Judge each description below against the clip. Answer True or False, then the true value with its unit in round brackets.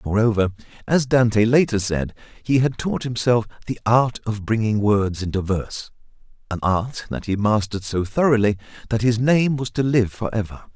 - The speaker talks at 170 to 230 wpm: False (160 wpm)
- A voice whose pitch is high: False (110 Hz)